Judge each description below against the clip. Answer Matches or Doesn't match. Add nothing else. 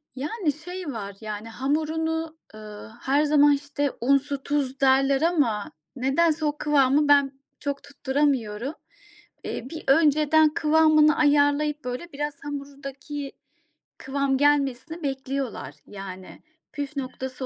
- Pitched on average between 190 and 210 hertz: Doesn't match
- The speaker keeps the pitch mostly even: Matches